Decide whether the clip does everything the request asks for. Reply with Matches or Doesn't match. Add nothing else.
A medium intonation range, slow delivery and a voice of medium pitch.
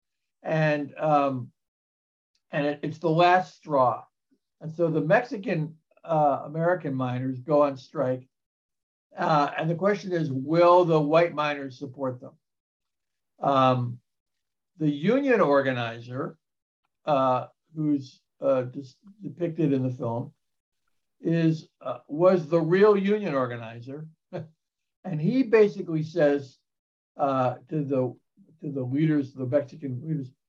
Matches